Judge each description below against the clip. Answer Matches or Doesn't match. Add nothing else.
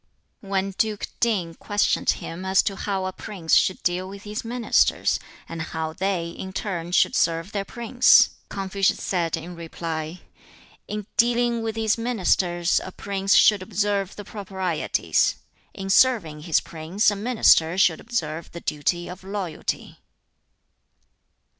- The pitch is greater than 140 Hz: Matches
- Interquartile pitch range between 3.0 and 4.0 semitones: Matches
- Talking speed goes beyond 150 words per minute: Doesn't match